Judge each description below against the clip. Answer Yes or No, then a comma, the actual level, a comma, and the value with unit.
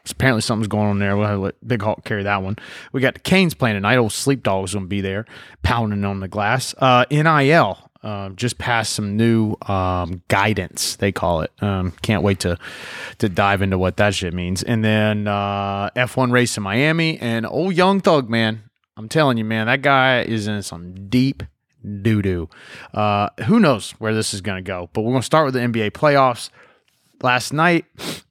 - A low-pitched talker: Yes, low, 110 Hz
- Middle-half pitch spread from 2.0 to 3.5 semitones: No, average, 4.1 semitones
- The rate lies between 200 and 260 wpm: Yes, fast, 205 wpm